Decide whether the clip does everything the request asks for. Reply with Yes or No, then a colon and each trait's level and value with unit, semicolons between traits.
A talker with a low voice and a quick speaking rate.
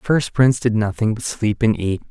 Yes: low, 110 Hz; fast, 255 wpm